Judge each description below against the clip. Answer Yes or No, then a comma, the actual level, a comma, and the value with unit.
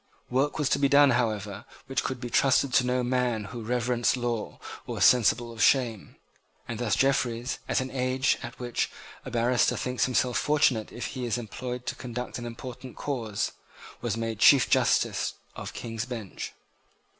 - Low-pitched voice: Yes, low, 125 Hz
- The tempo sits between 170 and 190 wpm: Yes, average, 180 wpm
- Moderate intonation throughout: No, narrow, 1.9 semitones